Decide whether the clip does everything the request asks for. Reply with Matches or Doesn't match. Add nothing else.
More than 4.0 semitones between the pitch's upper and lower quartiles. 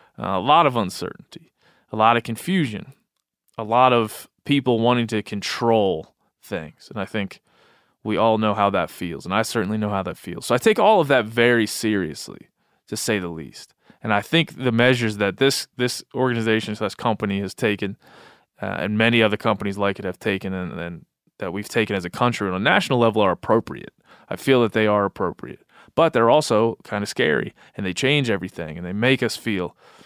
Doesn't match